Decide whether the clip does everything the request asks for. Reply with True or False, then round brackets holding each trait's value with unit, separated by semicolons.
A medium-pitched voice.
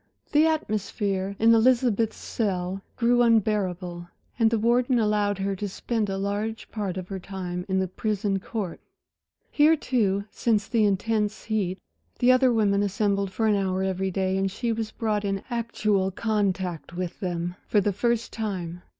False (205 Hz)